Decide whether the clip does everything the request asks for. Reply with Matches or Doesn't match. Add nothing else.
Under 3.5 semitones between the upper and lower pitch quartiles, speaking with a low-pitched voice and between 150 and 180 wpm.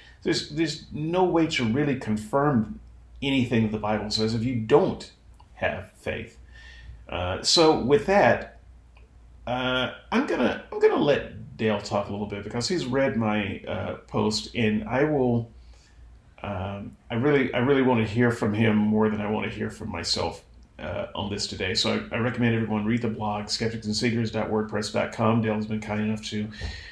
Matches